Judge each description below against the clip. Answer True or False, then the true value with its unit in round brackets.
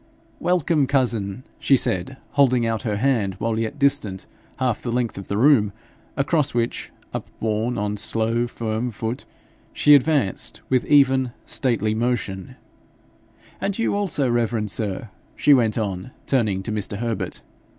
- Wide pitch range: False (3.9 semitones)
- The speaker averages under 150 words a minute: True (140 wpm)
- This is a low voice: True (115 Hz)